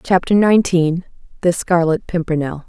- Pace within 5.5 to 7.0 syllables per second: No, 5.1 syllables/s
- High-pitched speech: No, medium, 175 Hz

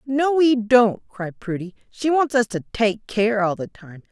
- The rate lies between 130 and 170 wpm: No, fast, 205 wpm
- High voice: Yes, high, 225 Hz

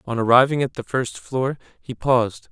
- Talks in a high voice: No, low, 125 Hz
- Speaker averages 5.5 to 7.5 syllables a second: No, 5.1 syllables/s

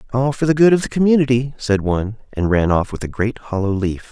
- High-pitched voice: No, low, 120 Hz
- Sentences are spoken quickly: Yes, fast, 250 wpm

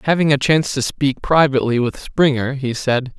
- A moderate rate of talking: Yes, average, 190 wpm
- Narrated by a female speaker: No, male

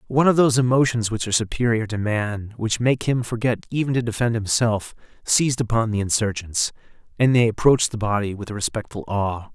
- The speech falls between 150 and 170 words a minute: No, average, 180 wpm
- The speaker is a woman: No, male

